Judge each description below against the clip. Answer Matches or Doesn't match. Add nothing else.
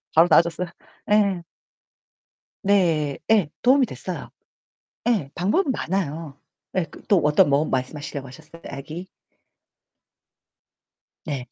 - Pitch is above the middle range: Doesn't match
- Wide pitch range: Doesn't match